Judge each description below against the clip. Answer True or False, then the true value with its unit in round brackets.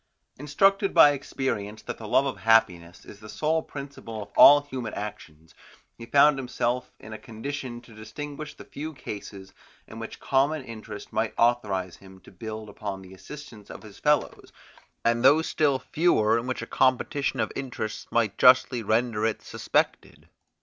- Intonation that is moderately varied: True (4.7 semitones)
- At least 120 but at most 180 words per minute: True (165 wpm)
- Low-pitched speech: True (115 Hz)